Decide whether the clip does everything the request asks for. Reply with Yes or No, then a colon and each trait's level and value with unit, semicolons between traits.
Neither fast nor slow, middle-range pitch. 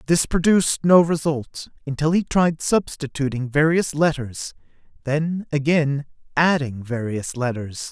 No: slow, 115 wpm; medium, 150 Hz